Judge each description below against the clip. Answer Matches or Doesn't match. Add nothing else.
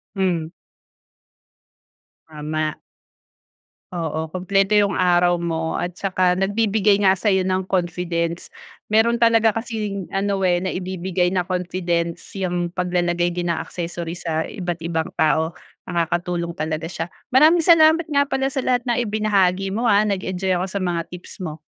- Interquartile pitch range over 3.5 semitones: Doesn't match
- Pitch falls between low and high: Matches